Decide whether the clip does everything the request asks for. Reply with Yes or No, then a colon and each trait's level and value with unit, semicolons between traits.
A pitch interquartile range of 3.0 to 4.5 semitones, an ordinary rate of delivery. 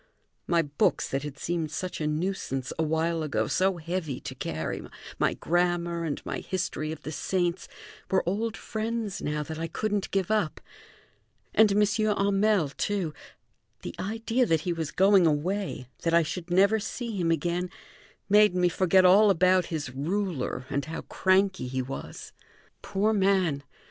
Yes: average, 4.1 semitones; average, 160 wpm